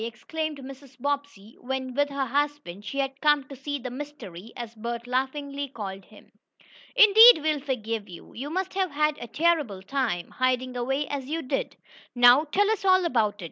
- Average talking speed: Yes, average, 180 wpm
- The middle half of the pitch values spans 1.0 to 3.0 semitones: No, average, 3.6 semitones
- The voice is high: Yes, very high, 270 Hz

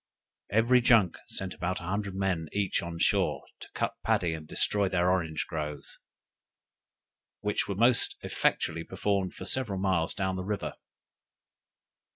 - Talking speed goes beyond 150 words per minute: No, average, 145 wpm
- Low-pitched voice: Yes, very low, 95 Hz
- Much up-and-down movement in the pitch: No, average, 3.1 semitones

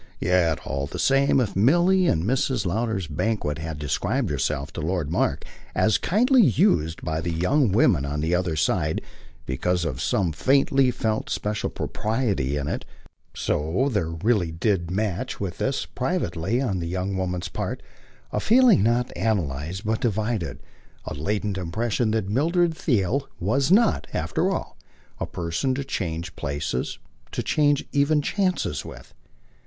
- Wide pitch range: Yes, wide, 7.6 semitones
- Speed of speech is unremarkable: Yes, average, 150 wpm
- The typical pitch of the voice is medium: No, low, 100 Hz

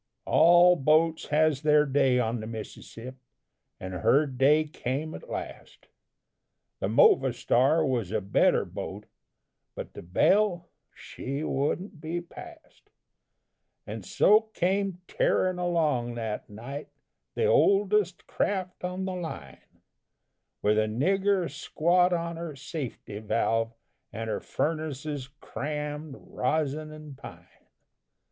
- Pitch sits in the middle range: Yes, medium, 155 Hz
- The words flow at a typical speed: No, slow, 115 wpm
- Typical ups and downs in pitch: No, wide, 5.7 semitones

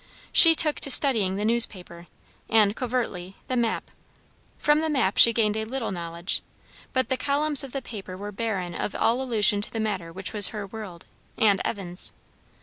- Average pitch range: Yes, average, 4.8 semitones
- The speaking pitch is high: Yes, high, 220 Hz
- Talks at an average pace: Yes, average, 180 wpm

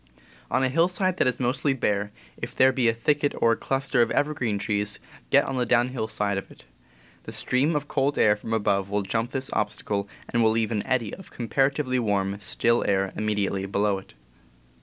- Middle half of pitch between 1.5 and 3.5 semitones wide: No, average, 4.5 semitones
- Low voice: Yes, low, 115 Hz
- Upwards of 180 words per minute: Yes, average, 200 wpm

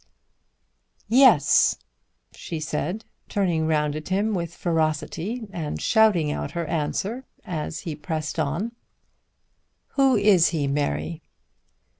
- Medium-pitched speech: Yes, medium, 165 Hz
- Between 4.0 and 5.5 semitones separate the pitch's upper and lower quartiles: Yes, average, 5.0 semitones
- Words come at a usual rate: No, slow, 110 wpm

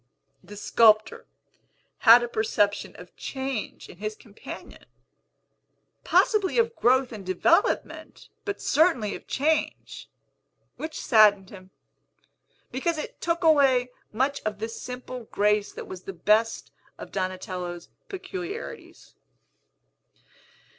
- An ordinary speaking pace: No, slow, 110 wpm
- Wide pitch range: Yes, wide, 6.8 semitones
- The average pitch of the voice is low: No, high, 230 Hz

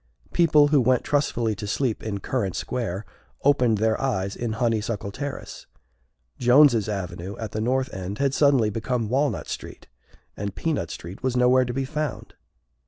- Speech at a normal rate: Yes, average, 160 wpm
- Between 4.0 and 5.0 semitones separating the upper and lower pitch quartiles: Yes, average, 4.3 semitones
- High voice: No, low, 120 Hz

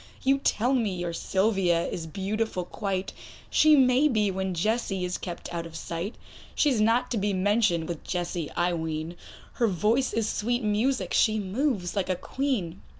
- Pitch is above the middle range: Yes, high, 200 Hz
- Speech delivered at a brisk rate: No, average, 175 wpm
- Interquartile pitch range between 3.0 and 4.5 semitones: No, average, 4.9 semitones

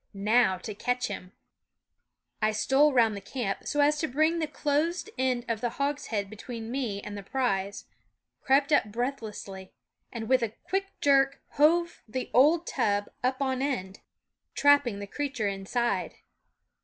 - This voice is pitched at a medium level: No, very high, 250 Hz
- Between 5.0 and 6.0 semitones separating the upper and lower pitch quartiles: Yes, wide, 5.4 semitones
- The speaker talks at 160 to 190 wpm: Yes, average, 170 wpm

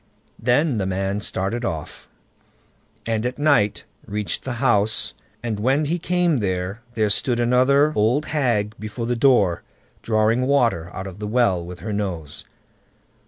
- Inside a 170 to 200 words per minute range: No, average, 150 wpm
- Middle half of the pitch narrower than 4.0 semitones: No, average, 4.3 semitones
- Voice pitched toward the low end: Yes, low, 110 Hz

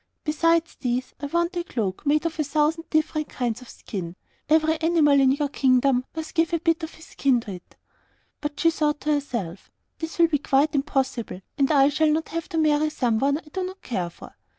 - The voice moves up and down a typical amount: Yes, average, 3.6 semitones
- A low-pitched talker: No, very high, 295 Hz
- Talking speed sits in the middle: No, fast, 210 wpm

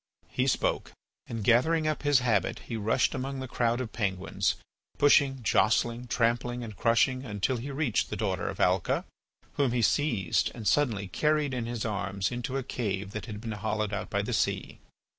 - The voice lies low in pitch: Yes, low, 120 Hz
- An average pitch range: Yes, average, 3.8 semitones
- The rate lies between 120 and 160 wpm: No, average, 180 wpm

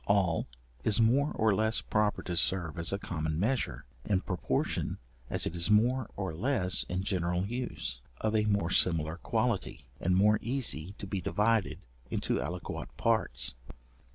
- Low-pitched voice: Yes, low, 100 Hz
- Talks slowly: No, average, 155 wpm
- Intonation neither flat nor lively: Yes, average, 4.0 semitones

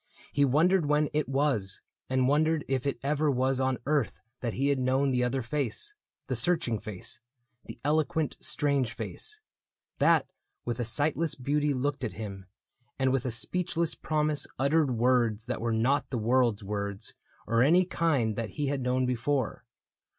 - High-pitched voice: No, low, 135 Hz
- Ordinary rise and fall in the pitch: Yes, average, 3.8 semitones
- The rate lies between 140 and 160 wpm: No, average, 170 wpm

